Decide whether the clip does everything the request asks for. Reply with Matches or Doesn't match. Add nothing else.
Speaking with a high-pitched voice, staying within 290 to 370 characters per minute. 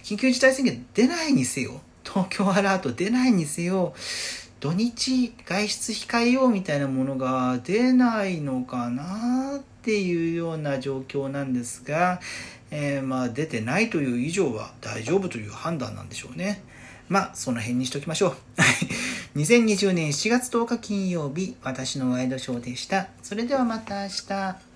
Doesn't match